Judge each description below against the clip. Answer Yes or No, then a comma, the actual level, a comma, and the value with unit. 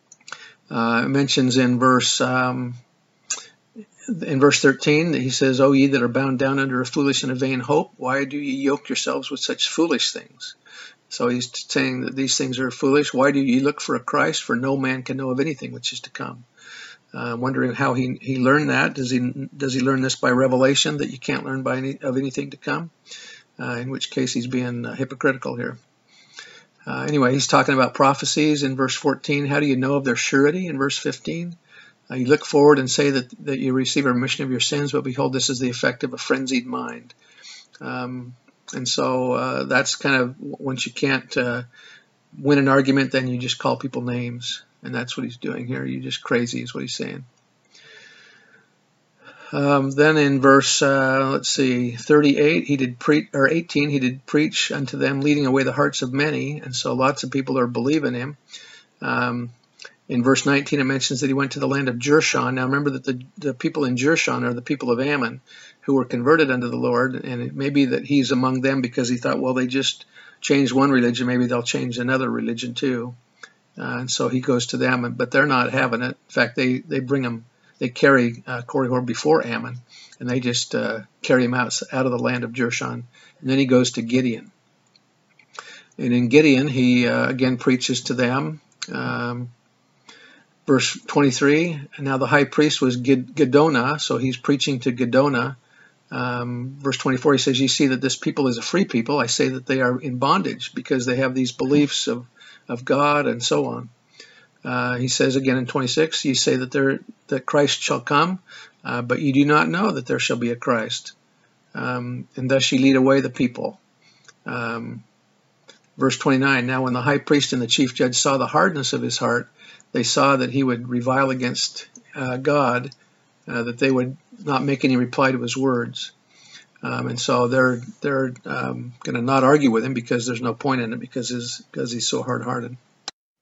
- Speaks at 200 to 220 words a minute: Yes, fast, 205 wpm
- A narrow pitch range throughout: Yes, narrow, 2.1 semitones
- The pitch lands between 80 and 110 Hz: No, low, 130 Hz